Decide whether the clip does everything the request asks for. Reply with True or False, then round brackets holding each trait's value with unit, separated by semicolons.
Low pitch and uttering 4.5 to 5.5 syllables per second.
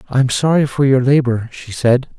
True (130 Hz; 5.2 syllables/s)